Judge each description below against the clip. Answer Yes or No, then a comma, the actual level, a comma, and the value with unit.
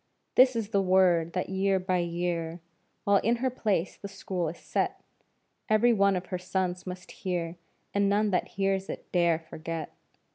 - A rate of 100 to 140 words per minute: No, average, 175 wpm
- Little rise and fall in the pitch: Yes, narrow, 2.3 semitones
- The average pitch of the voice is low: No, medium, 185 Hz